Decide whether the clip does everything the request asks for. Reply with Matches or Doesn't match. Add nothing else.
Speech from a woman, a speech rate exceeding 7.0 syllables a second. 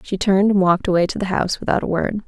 Matches